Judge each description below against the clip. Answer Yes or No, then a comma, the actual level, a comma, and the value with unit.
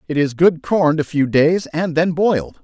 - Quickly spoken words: Yes, fast, 225 wpm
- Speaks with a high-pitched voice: No, medium, 160 Hz